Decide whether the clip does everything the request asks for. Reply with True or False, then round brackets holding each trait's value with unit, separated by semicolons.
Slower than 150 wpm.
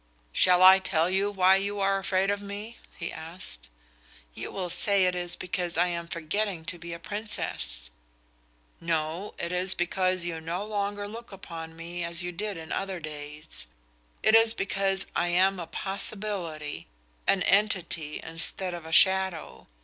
False (165 wpm)